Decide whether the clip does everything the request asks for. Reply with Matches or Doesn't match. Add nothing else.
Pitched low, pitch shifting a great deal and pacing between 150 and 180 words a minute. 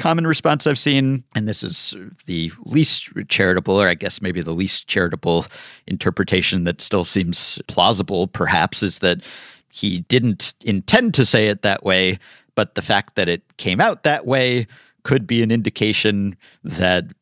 Matches